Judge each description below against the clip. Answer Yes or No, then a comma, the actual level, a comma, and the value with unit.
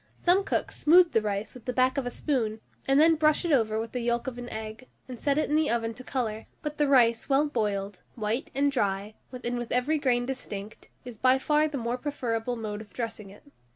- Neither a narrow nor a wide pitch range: Yes, average, 4.0 semitones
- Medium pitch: No, high, 245 Hz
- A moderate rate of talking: No, fast, 225 wpm